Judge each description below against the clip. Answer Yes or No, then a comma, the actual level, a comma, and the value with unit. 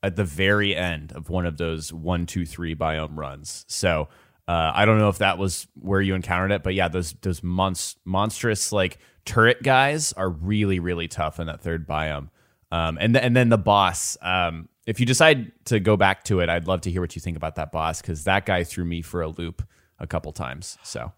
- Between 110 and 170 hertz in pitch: No, very low, 90 Hz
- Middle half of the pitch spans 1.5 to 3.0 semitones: No, average, 3.7 semitones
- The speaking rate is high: Yes, fast, 225 wpm